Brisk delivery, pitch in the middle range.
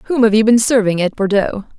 No: fast, 235 wpm; high, 215 Hz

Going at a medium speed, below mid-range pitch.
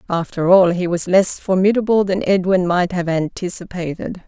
No: average, 155 wpm; medium, 180 Hz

